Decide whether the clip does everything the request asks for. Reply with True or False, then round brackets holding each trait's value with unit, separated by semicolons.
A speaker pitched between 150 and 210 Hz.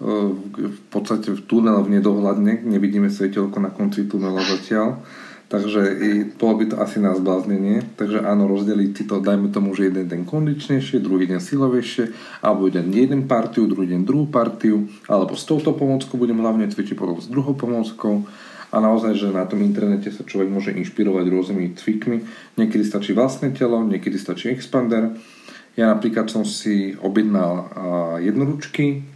False (105 Hz)